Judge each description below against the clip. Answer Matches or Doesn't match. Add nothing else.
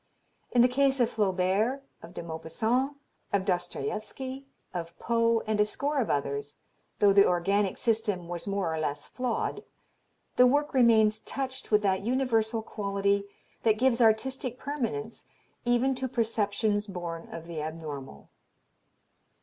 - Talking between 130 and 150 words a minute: Matches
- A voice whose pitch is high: Matches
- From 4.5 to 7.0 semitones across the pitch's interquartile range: Matches